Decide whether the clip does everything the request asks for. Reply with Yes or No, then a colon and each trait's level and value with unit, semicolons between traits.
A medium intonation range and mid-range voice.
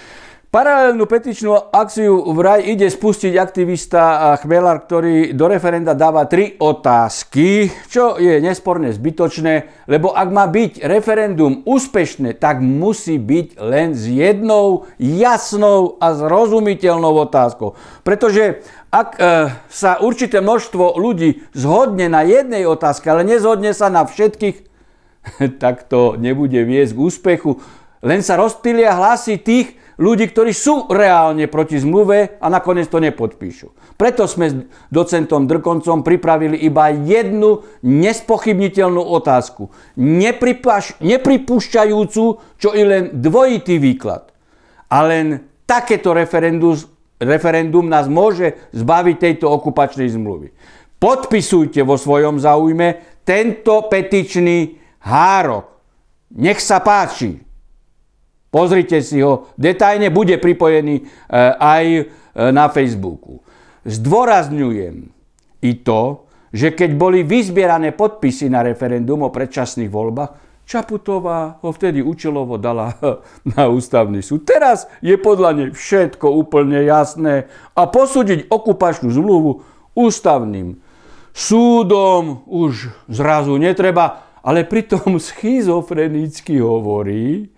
No: wide, 6.0 semitones; medium, 170 Hz